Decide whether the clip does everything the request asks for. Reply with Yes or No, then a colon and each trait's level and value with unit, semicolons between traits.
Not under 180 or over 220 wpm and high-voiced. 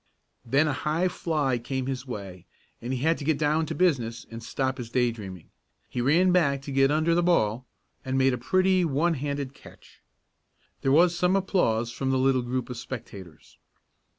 No: average, 190 wpm; low, 135 Hz